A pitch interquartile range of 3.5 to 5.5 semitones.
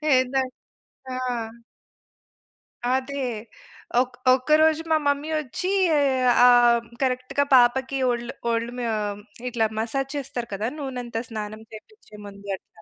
No: average, 2.8 semitones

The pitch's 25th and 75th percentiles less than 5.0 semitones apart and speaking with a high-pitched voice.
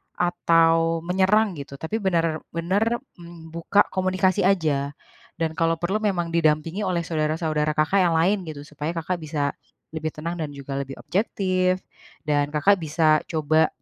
No: average, 3.1 semitones; medium, 165 Hz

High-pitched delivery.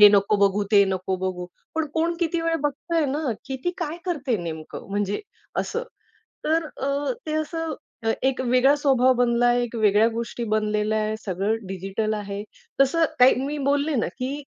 Yes: high, 245 Hz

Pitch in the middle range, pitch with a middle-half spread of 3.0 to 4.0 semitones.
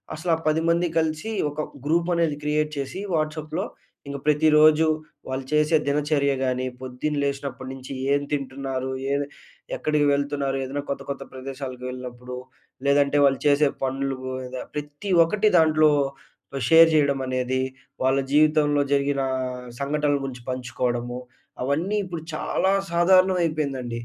No: medium, 145 Hz; narrow, 2.6 semitones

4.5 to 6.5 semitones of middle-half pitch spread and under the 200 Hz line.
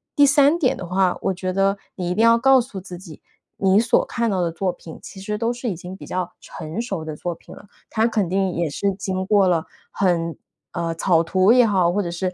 No: average, 3.6 semitones; high, 190 Hz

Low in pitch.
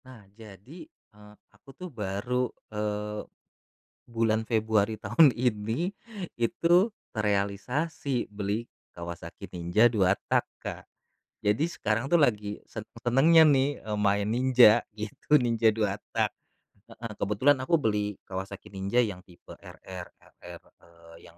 Yes: low, 105 Hz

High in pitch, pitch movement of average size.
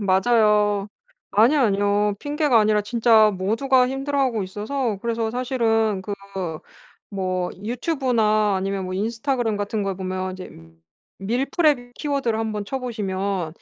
Yes: high, 220 Hz; average, 3.8 semitones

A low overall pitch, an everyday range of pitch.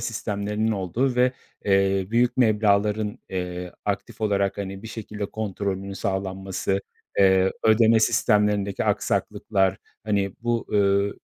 No: low, 100 Hz; narrow, 2.1 semitones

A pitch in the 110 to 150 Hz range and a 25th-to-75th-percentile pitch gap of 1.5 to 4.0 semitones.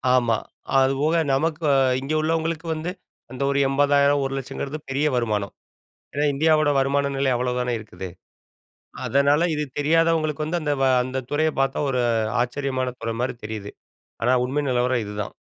Yes: medium, 140 Hz; average, 3.4 semitones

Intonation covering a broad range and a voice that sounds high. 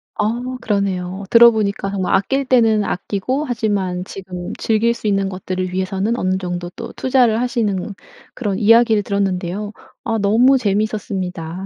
No: average, 3.3 semitones; high, 200 Hz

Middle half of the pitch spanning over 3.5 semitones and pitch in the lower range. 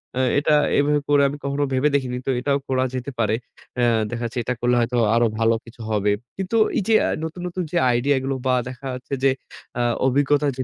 No: average, 2.9 semitones; low, 130 Hz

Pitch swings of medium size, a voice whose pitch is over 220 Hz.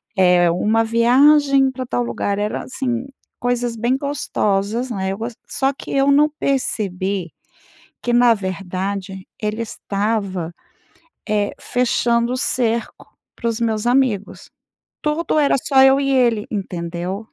Yes: average, 4.6 semitones; high, 230 Hz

